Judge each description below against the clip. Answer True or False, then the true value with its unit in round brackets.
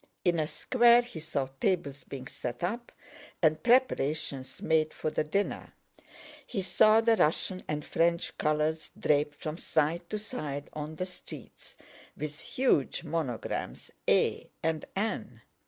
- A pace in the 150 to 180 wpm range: False (140 wpm)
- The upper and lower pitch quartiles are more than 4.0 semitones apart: True (4.6 semitones)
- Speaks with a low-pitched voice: False (160 Hz)